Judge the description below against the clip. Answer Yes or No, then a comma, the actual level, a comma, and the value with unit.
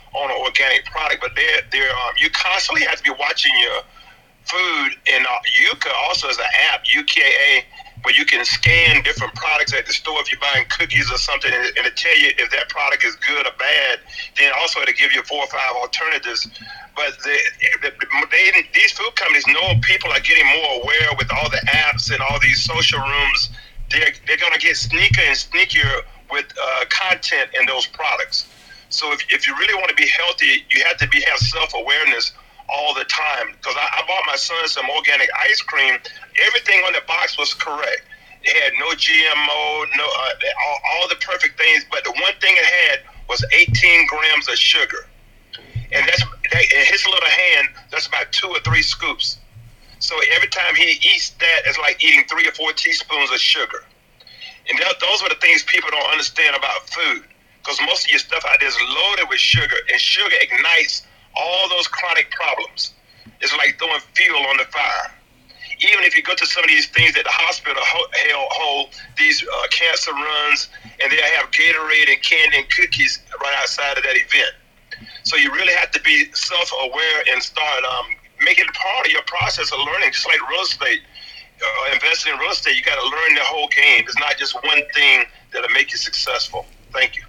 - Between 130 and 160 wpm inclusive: No, average, 200 wpm